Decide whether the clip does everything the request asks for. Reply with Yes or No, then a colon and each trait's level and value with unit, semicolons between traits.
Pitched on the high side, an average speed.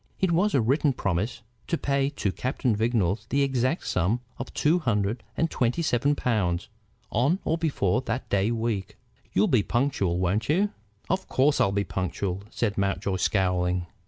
No: low, 115 Hz; average, 165 wpm